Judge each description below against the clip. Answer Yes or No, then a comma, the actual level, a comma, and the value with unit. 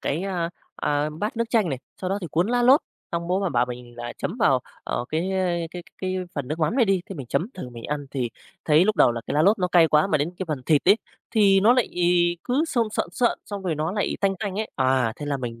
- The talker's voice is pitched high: No, medium, 170 Hz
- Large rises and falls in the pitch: Yes, wide, 5.8 semitones